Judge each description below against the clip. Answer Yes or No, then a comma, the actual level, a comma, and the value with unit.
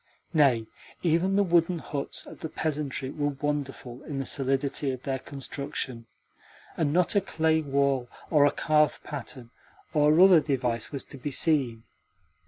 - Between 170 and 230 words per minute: No, average, 155 wpm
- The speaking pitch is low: No, medium, 145 Hz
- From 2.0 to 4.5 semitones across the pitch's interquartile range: Yes, average, 2.9 semitones